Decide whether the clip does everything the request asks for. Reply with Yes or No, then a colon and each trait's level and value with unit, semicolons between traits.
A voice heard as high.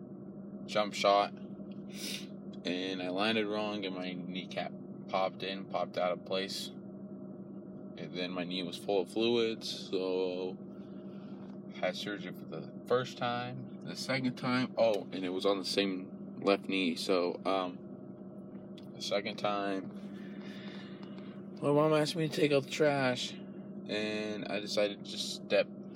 No: low, 125 Hz